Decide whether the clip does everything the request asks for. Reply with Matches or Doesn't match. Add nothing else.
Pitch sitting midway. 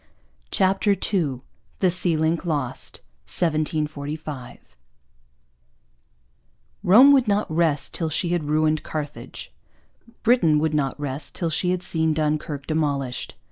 Matches